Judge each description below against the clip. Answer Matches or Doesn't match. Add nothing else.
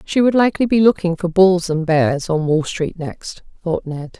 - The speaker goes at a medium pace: Doesn't match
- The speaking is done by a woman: Matches